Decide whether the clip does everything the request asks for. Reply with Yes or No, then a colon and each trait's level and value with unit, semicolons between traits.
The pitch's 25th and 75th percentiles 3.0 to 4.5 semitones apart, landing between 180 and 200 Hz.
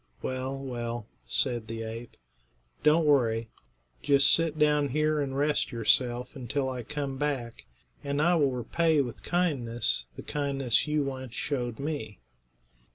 No: average, 3.6 semitones; low, 135 Hz